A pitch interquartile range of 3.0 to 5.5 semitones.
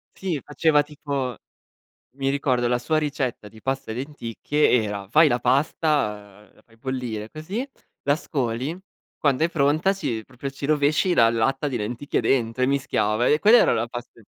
Yes: average, 4.3 semitones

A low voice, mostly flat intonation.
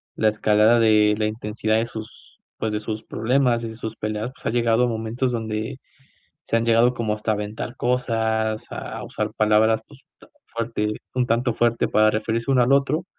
Yes: low, 110 Hz; narrow, 1.7 semitones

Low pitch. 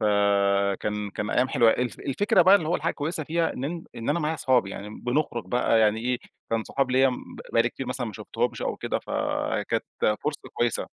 Yes: low, 125 Hz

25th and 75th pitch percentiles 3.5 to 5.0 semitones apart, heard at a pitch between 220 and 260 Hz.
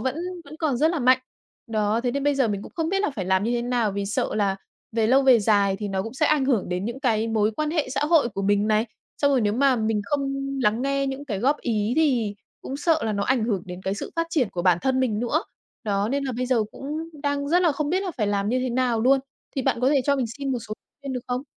Yes: average, 4.6 semitones; high, 245 Hz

